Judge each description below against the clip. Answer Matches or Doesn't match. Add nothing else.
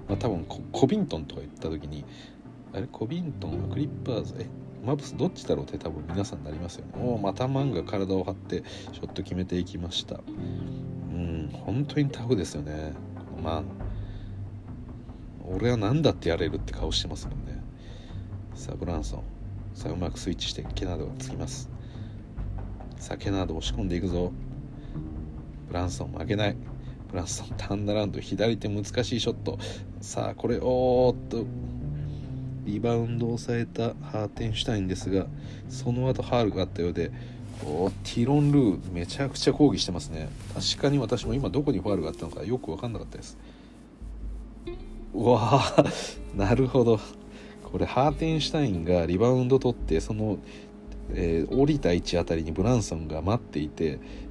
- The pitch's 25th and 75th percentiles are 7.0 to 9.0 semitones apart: Doesn't match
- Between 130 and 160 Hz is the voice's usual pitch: Doesn't match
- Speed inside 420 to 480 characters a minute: Doesn't match